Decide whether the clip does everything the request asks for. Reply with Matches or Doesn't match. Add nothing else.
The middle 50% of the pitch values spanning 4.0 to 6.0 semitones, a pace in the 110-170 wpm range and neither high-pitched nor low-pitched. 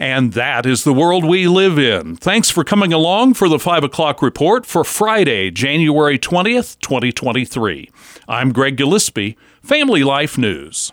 Matches